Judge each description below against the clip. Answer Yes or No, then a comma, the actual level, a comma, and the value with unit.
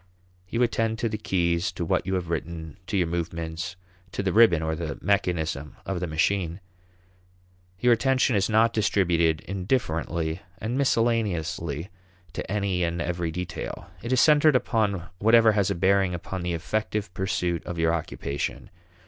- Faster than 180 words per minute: No, average, 155 wpm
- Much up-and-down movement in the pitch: No, average, 4.4 semitones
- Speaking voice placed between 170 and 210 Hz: No, very low, 90 Hz